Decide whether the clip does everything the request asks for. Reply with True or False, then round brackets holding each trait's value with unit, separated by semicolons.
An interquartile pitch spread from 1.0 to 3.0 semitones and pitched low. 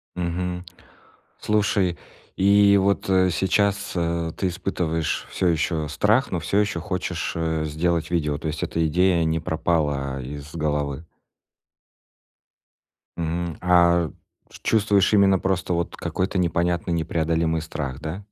True (2.7 semitones; 85 Hz)